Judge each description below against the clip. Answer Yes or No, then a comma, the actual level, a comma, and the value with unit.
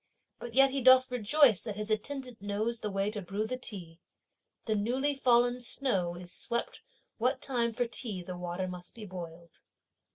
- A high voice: Yes, high, 220 Hz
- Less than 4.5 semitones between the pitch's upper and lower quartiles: No, average, 4.9 semitones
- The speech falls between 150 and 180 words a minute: Yes, average, 175 wpm